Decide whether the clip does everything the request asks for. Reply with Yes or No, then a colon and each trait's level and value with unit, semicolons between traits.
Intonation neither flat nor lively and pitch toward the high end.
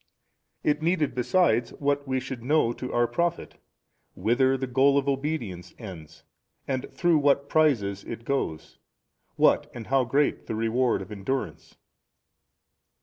No: average, 3.6 semitones; low, 130 Hz